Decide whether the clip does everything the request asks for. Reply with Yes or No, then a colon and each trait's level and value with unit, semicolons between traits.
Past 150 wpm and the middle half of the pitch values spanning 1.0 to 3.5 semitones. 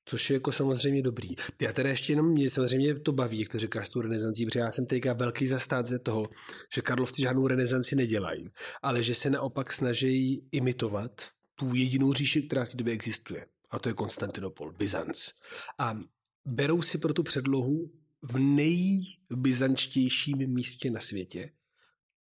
Yes: average, 165 wpm; narrow, 2.5 semitones